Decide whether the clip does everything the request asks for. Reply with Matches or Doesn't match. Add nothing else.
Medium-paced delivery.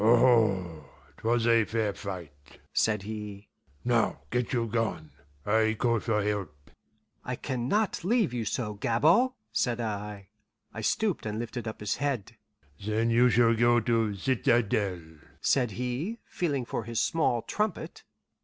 Matches